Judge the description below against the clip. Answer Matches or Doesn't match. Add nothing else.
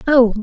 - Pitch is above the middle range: Matches